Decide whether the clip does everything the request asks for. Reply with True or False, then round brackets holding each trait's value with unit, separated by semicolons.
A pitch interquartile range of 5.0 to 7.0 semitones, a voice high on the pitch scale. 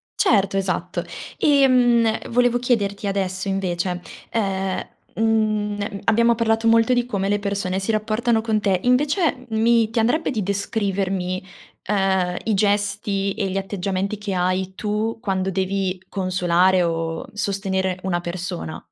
False (2.9 semitones; 200 Hz)